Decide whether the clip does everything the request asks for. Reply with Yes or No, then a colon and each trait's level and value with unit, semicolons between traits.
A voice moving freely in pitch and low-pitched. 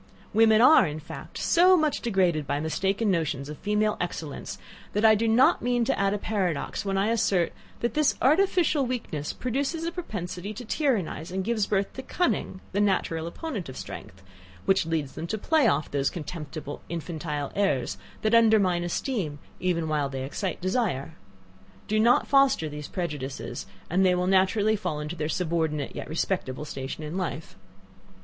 No: wide, 6.1 semitones; medium, 185 Hz